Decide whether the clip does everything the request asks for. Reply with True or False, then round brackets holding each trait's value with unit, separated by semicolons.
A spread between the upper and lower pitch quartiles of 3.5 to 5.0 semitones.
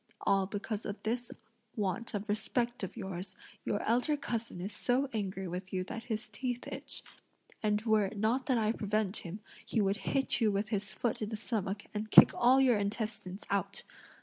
False (2.8 semitones)